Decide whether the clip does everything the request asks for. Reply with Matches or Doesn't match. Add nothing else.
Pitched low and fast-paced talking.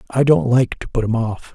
Matches